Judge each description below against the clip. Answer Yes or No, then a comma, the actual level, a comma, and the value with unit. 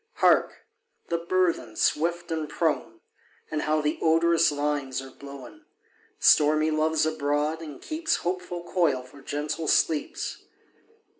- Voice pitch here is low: No, medium, 155 Hz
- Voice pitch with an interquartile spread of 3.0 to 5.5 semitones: No, narrow, 2.5 semitones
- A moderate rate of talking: No, slow, 125 wpm